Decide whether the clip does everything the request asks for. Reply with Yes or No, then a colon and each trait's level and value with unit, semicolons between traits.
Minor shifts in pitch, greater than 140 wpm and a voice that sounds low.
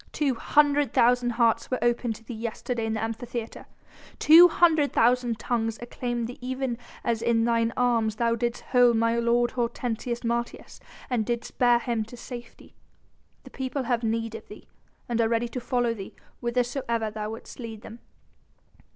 No: narrow, 1.4 semitones; average, 170 wpm; high, 235 Hz